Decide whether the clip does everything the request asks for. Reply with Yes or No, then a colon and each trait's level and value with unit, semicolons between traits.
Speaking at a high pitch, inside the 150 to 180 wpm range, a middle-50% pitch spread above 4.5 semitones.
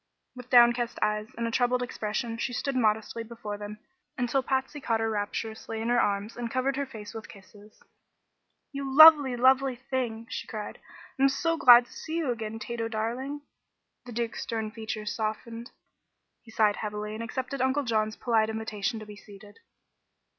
No: high, 230 Hz; average, 170 wpm; average, 3.0 semitones